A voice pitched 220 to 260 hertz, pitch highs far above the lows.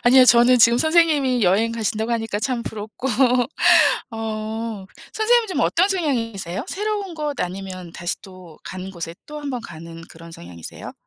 Yes: high, 225 Hz; wide, 6.8 semitones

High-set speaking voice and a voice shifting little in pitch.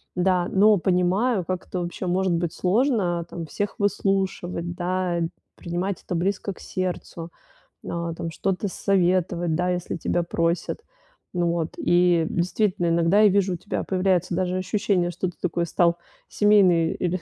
No: medium, 180 Hz; narrow, 1.9 semitones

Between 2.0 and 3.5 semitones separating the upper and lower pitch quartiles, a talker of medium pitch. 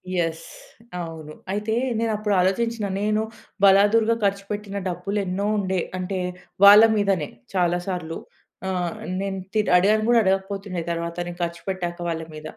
No: average, 2.9 semitones; high, 195 Hz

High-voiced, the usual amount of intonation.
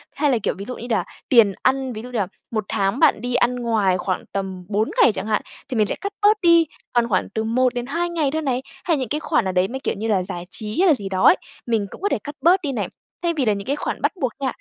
No: high, 240 Hz; wide, 5.7 semitones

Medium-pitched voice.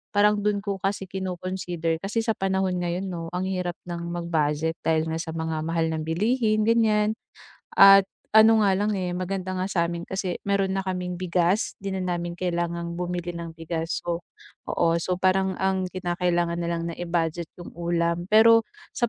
Yes: medium, 180 Hz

